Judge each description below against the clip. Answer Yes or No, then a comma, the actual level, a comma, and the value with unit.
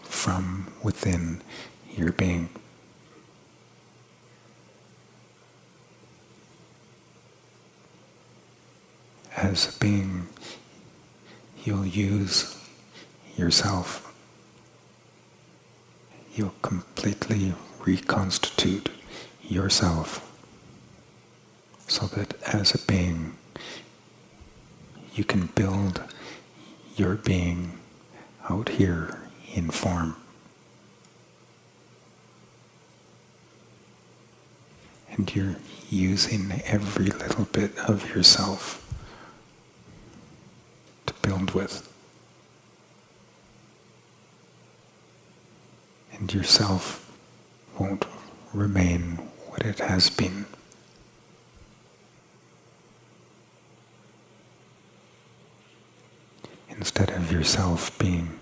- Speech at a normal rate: No, slow, 50 wpm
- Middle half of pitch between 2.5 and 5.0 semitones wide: Yes, average, 2.9 semitones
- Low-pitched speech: Yes, very low, 95 Hz